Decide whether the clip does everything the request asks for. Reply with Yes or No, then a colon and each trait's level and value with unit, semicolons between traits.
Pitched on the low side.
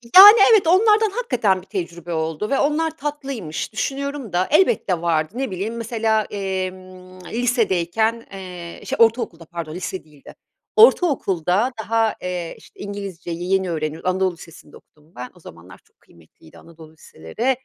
No: high, 190 Hz